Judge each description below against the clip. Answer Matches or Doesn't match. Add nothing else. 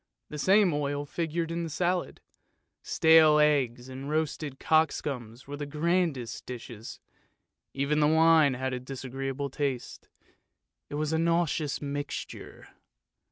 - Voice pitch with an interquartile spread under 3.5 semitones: Matches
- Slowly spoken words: Matches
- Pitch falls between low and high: Matches